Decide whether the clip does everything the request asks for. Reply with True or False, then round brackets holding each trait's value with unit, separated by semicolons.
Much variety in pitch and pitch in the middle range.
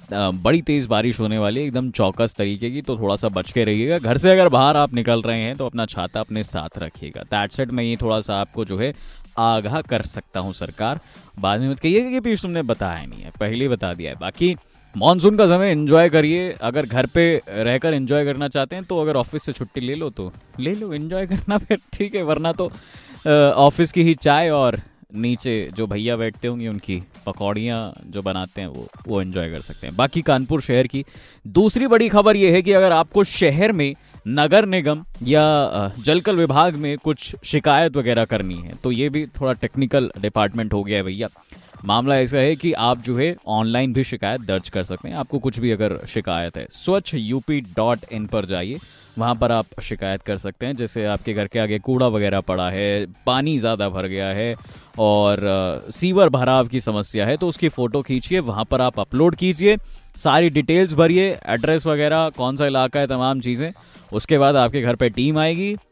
False (6.4 semitones; 125 Hz)